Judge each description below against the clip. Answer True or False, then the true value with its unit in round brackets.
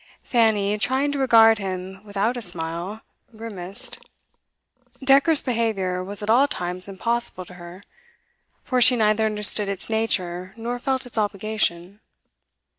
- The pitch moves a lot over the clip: False (3.9 semitones)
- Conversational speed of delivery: False (130 wpm)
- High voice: True (210 Hz)